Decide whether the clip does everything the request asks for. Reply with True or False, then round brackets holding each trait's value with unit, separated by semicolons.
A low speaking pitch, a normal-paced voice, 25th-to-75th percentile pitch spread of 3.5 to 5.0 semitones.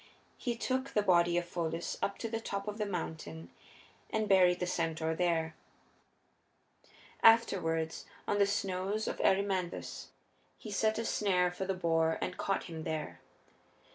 False (185 Hz; 150 wpm; 3.9 semitones)